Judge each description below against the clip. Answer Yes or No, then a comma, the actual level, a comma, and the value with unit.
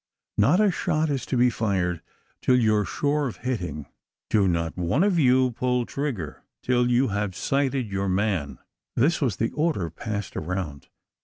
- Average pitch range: No, wide, 6.2 semitones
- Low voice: Yes, low, 115 Hz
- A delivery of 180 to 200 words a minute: No, average, 170 wpm